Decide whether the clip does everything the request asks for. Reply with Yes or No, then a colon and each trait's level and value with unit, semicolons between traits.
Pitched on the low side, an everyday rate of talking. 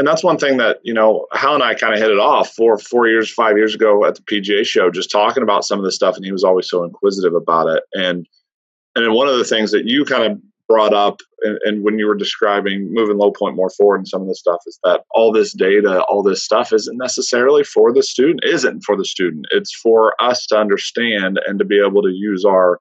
No: low, 115 Hz; fast, 255 wpm